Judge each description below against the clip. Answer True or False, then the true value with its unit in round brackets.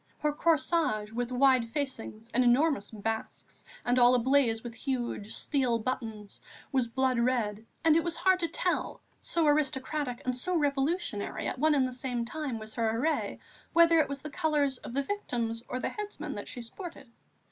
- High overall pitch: True (255 Hz)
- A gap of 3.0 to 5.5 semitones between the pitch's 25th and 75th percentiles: True (4.5 semitones)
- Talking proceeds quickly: False (180 wpm)